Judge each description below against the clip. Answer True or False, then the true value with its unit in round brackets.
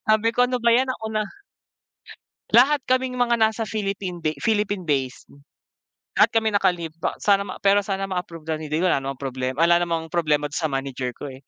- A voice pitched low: False (185 Hz)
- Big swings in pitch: True (6.2 semitones)